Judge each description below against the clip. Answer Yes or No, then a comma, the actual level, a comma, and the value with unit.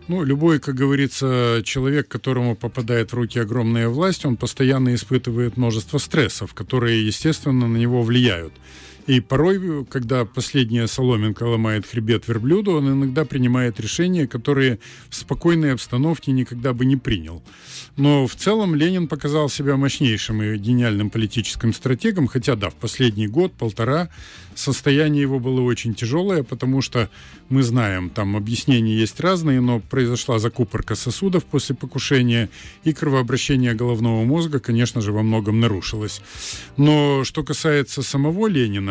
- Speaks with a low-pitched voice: Yes, low, 125 Hz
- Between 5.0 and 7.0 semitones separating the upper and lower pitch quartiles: No, average, 3.4 semitones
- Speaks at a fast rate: No, average, 140 wpm